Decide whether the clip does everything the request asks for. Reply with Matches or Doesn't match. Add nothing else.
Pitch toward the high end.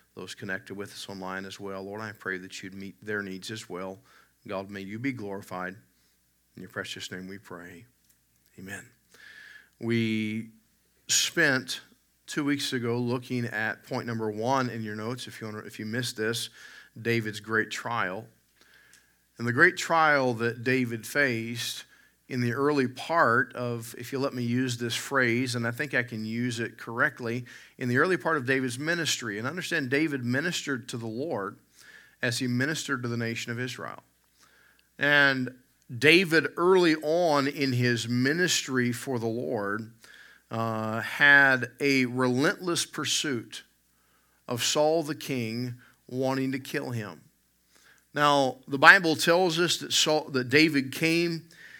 Doesn't match